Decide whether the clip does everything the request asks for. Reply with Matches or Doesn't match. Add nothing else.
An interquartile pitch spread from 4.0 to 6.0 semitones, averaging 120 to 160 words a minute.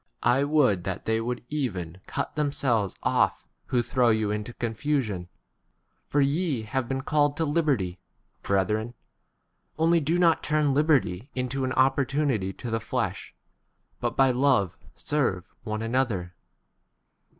Matches